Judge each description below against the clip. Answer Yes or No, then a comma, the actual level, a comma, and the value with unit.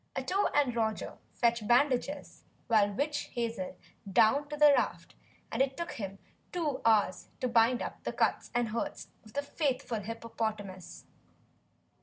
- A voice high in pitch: Yes, high, 235 Hz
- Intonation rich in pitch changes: No, average, 4.6 semitones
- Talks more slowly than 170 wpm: Yes, average, 145 wpm